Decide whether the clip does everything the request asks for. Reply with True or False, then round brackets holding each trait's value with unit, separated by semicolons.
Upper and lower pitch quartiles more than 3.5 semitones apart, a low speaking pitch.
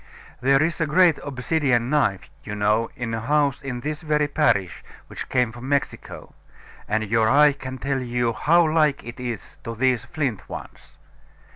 True (4.4 semitones; 130 Hz)